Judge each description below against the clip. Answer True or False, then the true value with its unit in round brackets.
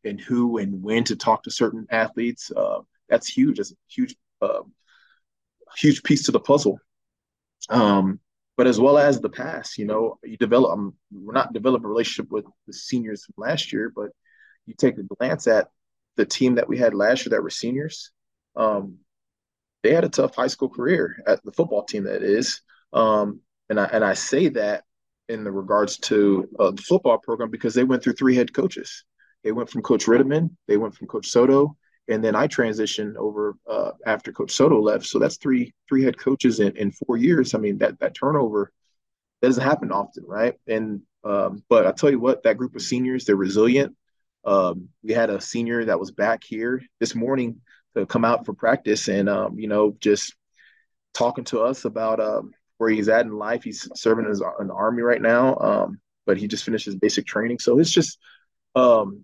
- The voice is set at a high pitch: False (120 Hz)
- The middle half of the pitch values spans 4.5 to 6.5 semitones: True (4.8 semitones)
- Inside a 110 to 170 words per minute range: False (200 wpm)